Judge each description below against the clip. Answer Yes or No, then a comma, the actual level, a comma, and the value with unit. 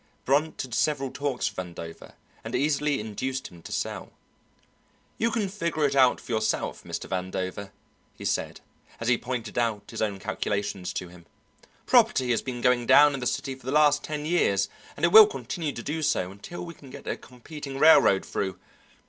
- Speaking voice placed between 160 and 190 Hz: No, low, 130 Hz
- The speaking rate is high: No, average, 190 wpm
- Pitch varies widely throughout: Yes, wide, 6.2 semitones